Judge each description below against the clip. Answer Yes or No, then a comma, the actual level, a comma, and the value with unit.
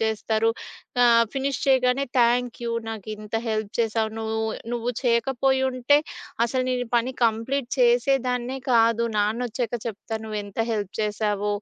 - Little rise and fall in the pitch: Yes, narrow, 2.3 semitones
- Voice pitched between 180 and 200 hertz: No, high, 235 Hz